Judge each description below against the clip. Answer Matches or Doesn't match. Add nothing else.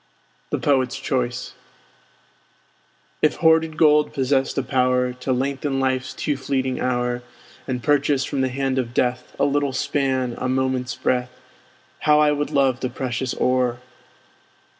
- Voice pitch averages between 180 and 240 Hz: Doesn't match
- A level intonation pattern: Matches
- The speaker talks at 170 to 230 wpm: Doesn't match